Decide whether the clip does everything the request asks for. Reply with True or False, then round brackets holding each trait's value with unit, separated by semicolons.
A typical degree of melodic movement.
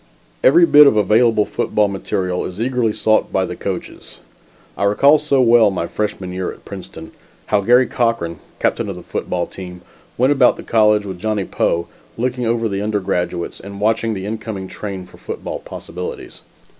True (3.6 semitones)